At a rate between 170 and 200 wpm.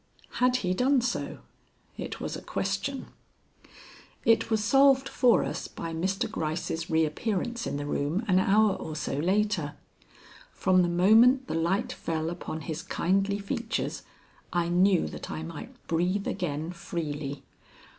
No: average, 145 wpm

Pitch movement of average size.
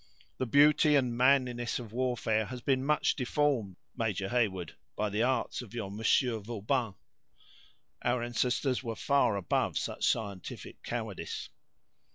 Yes: average, 3.2 semitones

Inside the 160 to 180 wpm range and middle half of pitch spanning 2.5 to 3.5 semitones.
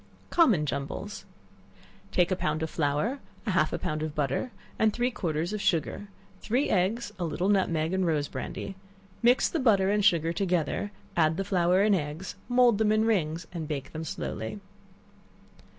No: average, 170 wpm; average, 5.2 semitones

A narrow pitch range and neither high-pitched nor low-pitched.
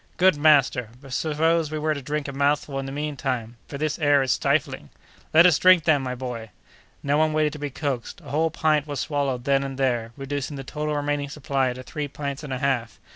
Yes: narrow, 2.2 semitones; medium, 145 Hz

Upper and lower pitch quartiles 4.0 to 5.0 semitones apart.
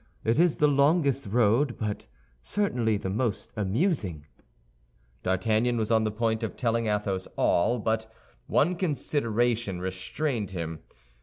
Yes: average, 4.5 semitones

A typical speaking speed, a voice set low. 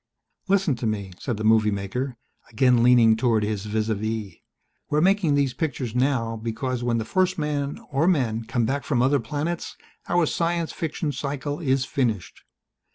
Yes: average, 170 wpm; low, 125 Hz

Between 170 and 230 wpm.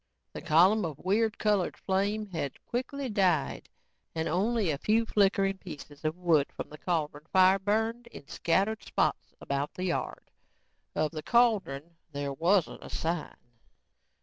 No: average, 150 wpm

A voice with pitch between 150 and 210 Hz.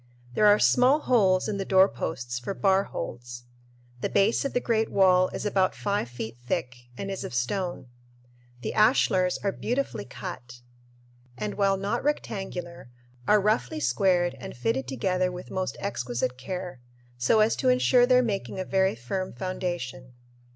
Yes: medium, 185 Hz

